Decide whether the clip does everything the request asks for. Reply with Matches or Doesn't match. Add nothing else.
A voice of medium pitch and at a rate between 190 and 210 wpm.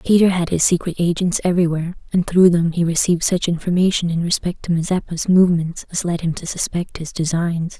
Matches